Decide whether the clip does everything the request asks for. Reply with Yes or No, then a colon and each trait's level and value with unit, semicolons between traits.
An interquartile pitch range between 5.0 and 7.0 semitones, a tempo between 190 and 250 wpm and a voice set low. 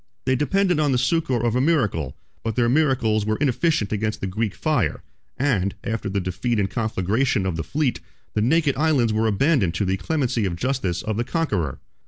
Yes: wide, 5.4 semitones; average, 195 wpm; low, 115 Hz